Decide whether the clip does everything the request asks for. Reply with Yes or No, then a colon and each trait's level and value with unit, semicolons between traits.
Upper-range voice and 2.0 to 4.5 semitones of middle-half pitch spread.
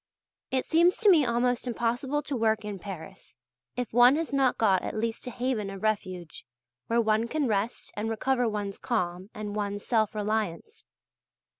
Yes: high, 225 Hz; average, 3.4 semitones